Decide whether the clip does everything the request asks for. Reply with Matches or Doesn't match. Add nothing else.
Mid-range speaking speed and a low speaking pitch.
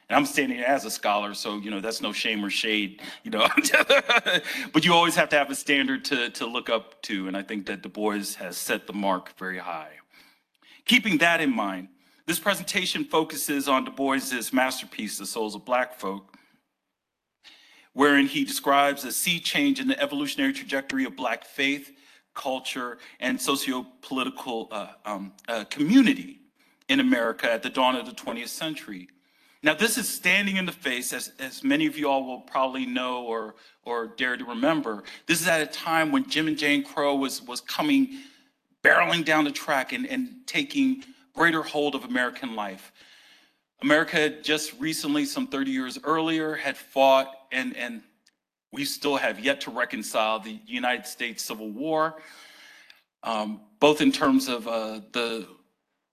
Doesn't match